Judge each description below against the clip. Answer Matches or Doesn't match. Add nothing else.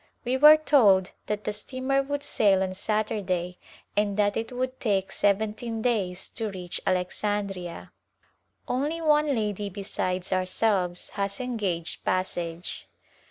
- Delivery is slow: Matches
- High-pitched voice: Matches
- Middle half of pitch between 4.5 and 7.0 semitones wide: Matches